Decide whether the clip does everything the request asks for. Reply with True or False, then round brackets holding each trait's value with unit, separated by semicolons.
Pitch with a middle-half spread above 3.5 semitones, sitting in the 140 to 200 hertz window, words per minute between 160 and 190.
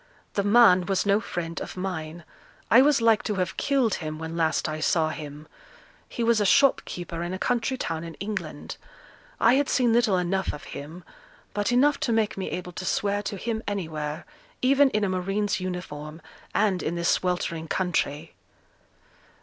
True (4.7 semitones; 185 Hz; 175 wpm)